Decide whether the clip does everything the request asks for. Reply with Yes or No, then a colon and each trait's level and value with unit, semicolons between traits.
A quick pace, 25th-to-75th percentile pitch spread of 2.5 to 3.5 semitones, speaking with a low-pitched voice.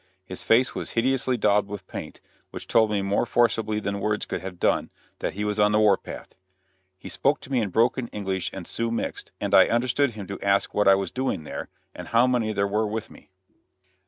Yes: fast, 220 wpm; average, 2.8 semitones; low, 105 Hz